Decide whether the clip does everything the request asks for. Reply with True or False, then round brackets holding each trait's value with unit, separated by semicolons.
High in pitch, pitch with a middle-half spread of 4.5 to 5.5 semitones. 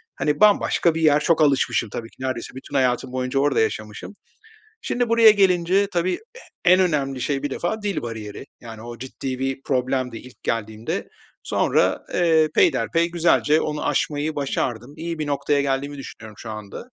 False (140 Hz; 4.9 semitones)